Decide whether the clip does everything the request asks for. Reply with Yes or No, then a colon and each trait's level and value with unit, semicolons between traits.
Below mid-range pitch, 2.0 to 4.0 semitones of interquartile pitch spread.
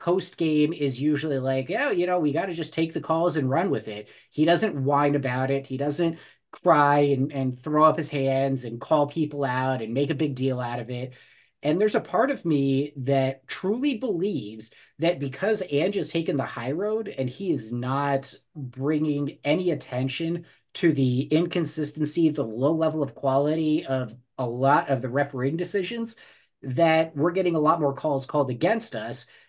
No: medium, 145 Hz; average, 3.5 semitones